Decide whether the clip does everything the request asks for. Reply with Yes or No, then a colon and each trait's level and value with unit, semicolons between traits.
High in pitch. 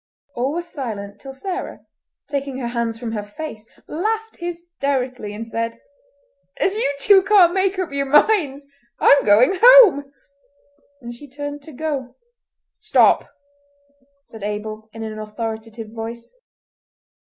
Yes: very high, 270 Hz